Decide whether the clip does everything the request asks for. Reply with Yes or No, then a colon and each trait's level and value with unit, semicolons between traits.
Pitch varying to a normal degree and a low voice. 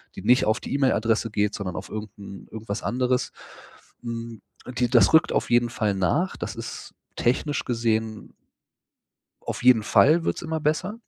Yes: average, 3.1 semitones; low, 115 Hz